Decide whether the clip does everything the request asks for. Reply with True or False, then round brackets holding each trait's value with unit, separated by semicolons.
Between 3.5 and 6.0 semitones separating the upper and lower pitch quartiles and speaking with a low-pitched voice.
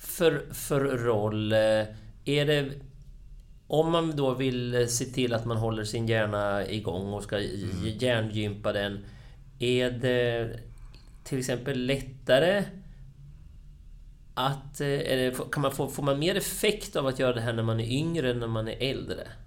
True (4.0 semitones; 125 Hz)